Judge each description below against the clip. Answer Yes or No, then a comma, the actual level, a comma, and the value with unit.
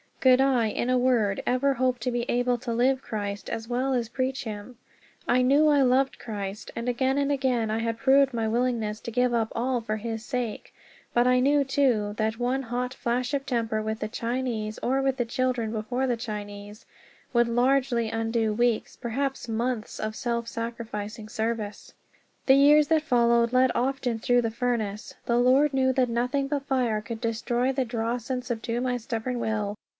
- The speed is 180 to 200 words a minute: Yes, average, 190 wpm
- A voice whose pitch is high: Yes, high, 240 Hz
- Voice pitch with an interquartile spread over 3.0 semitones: No, narrow, 2.5 semitones